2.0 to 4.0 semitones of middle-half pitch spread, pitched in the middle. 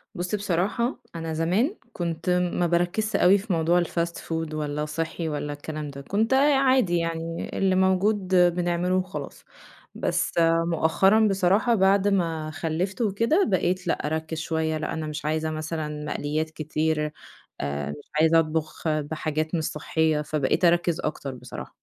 Yes: average, 3.2 semitones; medium, 165 Hz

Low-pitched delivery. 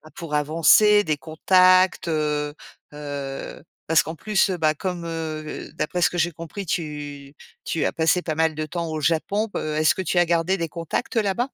No: medium, 165 Hz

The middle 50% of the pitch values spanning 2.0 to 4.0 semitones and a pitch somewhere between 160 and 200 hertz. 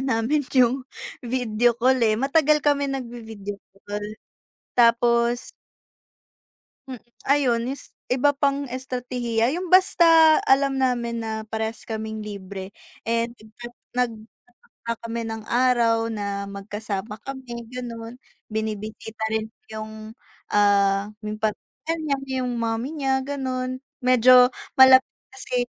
No: average, 3.1 semitones; high, 235 Hz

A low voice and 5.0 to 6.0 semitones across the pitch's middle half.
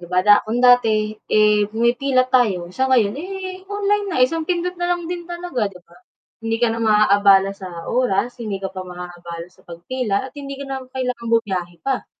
No: high, 230 Hz; wide, 5.6 semitones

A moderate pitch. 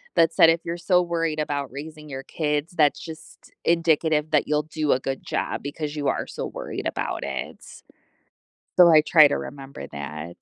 Yes: medium, 150 Hz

